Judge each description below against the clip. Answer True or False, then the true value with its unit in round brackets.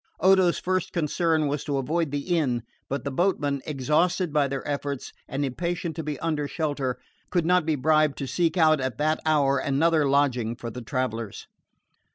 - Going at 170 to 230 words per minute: True (180 wpm)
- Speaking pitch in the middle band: True (150 Hz)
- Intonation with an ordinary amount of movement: True (3.2 semitones)